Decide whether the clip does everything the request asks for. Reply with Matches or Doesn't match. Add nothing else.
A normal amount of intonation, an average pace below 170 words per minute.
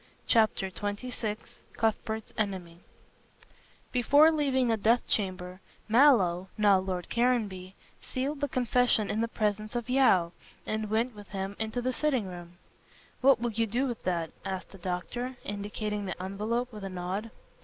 Matches